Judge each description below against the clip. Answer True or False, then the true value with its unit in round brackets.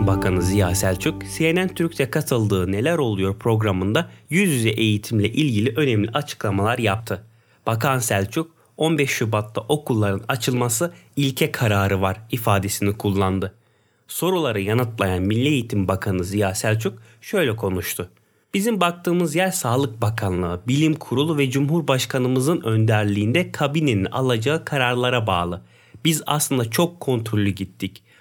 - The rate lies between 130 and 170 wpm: False (115 wpm)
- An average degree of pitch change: False (6.3 semitones)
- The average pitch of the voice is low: True (115 Hz)